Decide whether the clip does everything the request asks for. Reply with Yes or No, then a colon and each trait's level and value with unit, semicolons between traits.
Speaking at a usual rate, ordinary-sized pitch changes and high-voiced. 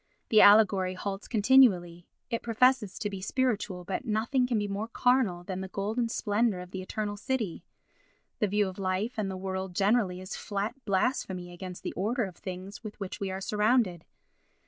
Yes: average, 180 wpm; average, 3.1 semitones; high, 200 Hz